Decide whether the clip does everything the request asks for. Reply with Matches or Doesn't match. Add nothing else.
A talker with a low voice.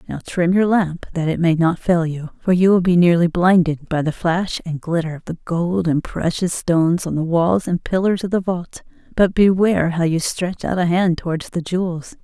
Doesn't match